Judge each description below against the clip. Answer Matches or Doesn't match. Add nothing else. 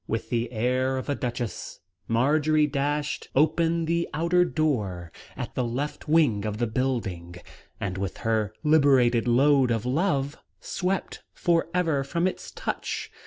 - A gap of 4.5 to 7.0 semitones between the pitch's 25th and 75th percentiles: Matches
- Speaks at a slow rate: Doesn't match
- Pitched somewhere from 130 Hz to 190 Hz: Matches